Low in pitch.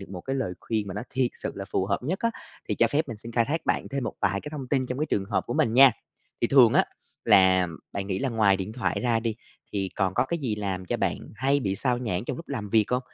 Yes: low, 115 Hz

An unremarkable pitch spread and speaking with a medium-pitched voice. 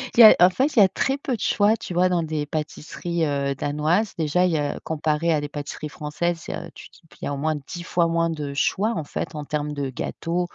Yes: average, 3.3 semitones; medium, 160 Hz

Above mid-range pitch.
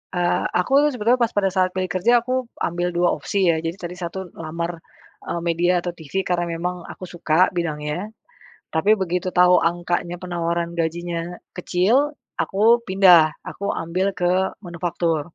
No: medium, 175 Hz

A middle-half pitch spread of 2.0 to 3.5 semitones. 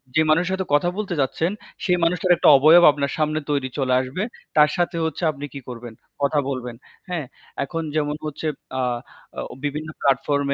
Yes: average, 3.2 semitones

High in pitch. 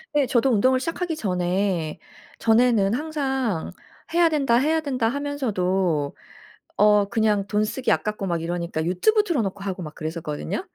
Yes: high, 215 Hz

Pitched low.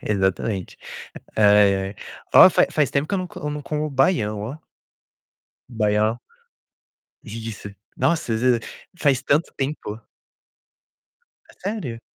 Yes: low, 120 Hz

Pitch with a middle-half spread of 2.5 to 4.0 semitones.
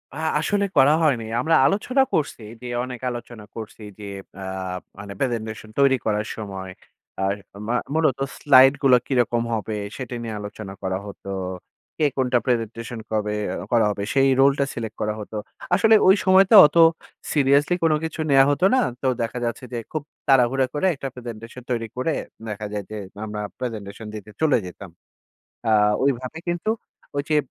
No: average, 4.4 semitones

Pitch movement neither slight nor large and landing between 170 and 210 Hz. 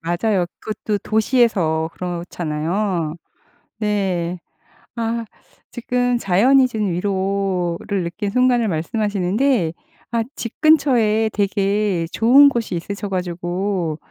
Yes: average, 4.3 semitones; high, 200 Hz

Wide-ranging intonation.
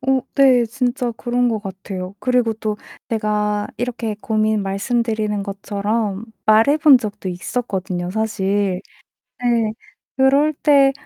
No: average, 3.4 semitones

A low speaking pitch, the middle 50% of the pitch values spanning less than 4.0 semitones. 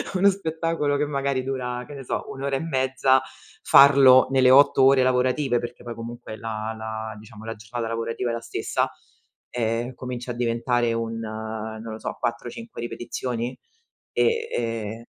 Yes: low, 120 Hz; average, 2.8 semitones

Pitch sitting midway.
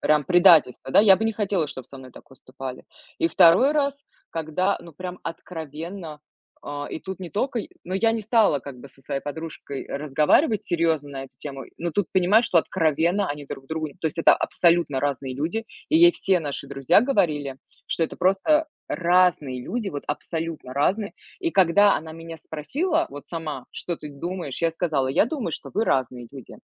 Yes: medium, 165 Hz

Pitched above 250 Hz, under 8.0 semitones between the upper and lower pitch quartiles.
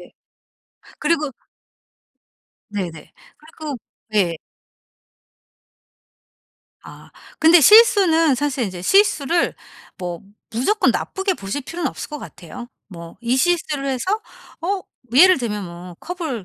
No: very high, 280 Hz; wide, 8.9 semitones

